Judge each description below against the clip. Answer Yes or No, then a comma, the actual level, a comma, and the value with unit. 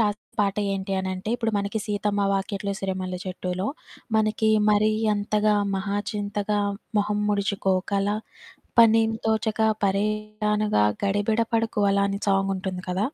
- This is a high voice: Yes, high, 205 Hz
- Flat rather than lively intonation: Yes, narrow, 1.5 semitones